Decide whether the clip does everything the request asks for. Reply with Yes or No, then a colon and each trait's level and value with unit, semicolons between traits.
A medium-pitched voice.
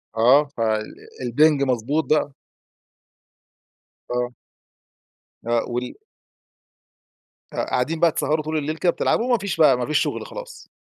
Yes: medium, 145 Hz